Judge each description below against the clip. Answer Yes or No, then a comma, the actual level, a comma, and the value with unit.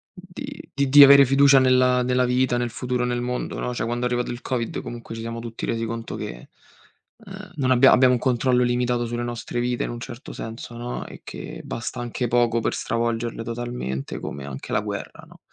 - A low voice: Yes, low, 120 Hz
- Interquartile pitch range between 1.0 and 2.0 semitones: Yes, narrow, 1.4 semitones